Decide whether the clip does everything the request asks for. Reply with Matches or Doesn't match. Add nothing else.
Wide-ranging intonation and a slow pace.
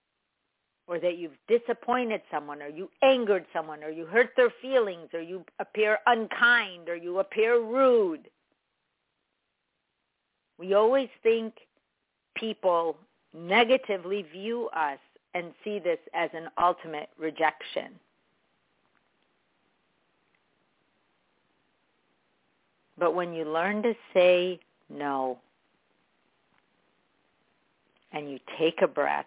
Matches